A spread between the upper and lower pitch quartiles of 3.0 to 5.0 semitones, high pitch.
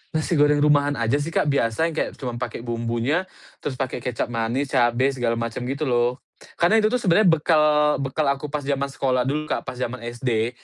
No: average, 3.7 semitones; low, 135 Hz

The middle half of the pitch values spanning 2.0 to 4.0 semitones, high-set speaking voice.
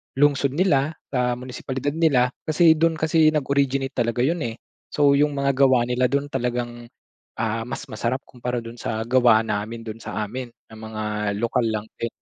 No: average, 3.5 semitones; low, 125 Hz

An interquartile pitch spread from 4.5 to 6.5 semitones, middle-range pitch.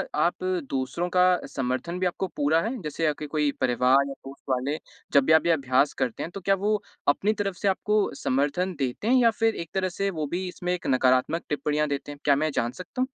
Yes: average, 5.3 semitones; medium, 155 Hz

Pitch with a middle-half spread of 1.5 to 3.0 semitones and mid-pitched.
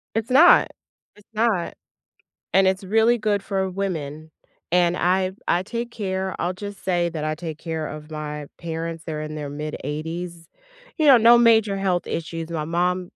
No: average, 3.8 semitones; medium, 180 Hz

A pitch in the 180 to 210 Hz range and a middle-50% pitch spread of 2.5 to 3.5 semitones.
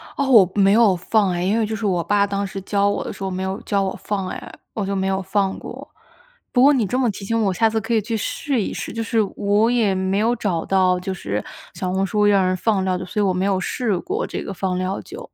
Yes: high, 200 Hz; average, 2.8 semitones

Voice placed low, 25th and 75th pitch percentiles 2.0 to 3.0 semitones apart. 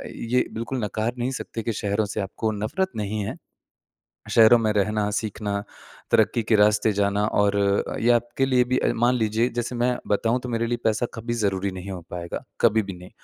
Yes: low, 110 Hz; average, 2.7 semitones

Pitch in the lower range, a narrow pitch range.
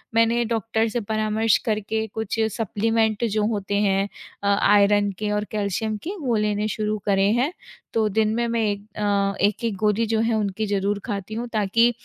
No: high, 215 Hz; narrow, 1.8 semitones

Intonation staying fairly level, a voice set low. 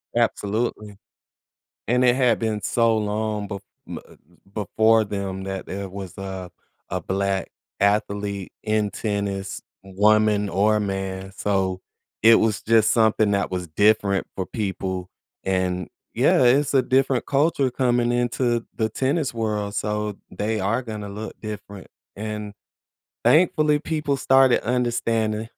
No: average, 3.0 semitones; low, 105 Hz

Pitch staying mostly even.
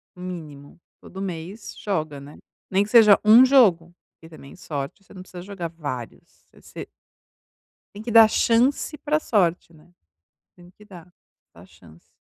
No: average, 5.1 semitones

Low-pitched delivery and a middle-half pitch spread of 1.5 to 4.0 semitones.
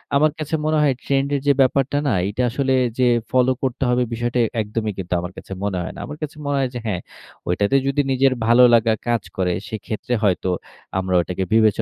No: low, 120 Hz; average, 4.8 semitones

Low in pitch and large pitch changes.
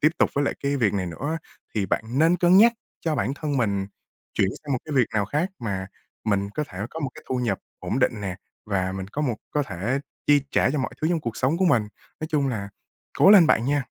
Yes: low, 130 Hz; wide, 6.8 semitones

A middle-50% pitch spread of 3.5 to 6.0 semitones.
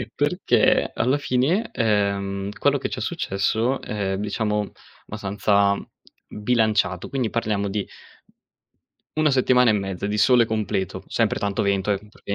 No: average, 2.8 semitones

